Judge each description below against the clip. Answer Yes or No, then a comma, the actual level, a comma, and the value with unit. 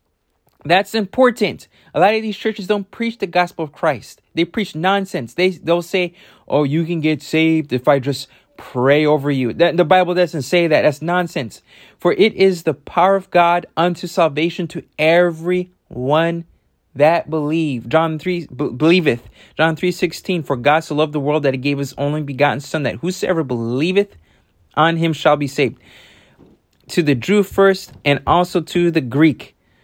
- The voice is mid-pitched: Yes, medium, 165 Hz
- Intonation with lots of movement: No, average, 3.6 semitones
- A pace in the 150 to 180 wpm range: Yes, average, 175 wpm